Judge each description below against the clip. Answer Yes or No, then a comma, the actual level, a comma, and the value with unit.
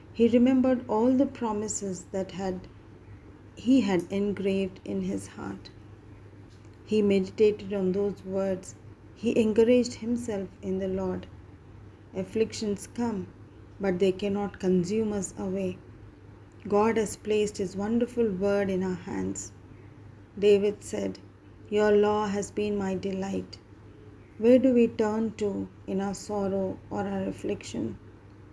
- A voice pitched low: No, high, 190 Hz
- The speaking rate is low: Yes, slow, 125 wpm